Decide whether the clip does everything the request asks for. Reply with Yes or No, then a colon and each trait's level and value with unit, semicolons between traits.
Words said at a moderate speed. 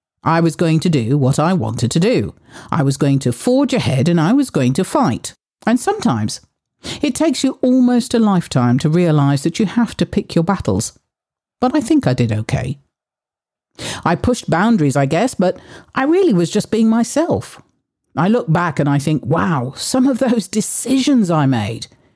Yes: average, 190 wpm